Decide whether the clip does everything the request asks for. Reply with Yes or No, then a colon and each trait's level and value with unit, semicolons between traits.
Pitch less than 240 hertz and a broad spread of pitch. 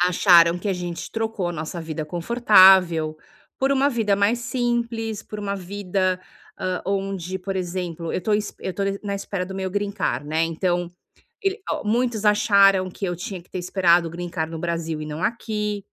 No: high, 190 Hz; average, 3.2 semitones